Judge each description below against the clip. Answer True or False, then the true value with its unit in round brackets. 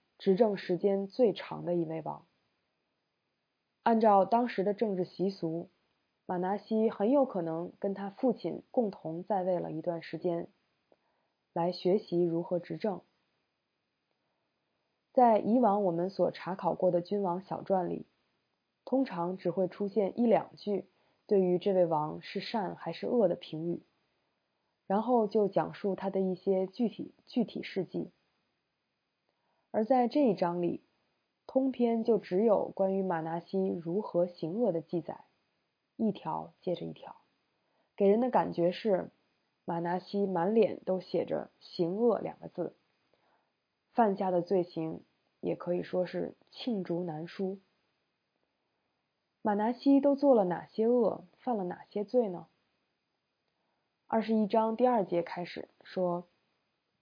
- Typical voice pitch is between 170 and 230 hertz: True (190 Hz)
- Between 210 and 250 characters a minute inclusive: False (195 characters per minute)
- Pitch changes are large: False (3.9 semitones)